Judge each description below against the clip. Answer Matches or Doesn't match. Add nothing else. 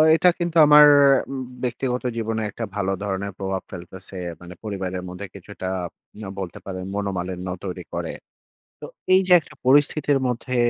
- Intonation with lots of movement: Matches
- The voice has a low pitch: Matches